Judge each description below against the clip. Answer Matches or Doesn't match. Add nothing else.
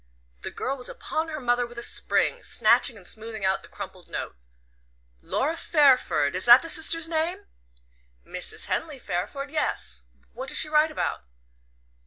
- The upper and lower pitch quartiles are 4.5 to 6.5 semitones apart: Matches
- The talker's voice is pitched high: Matches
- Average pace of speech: Matches